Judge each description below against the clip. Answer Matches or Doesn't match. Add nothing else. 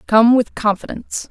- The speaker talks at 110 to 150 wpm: Matches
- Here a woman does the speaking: Matches